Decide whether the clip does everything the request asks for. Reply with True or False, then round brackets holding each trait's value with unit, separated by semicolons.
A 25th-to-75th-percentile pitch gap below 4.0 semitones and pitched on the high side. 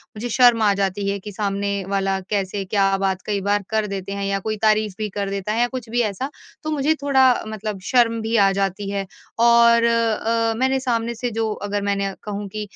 True (2.7 semitones; 210 Hz)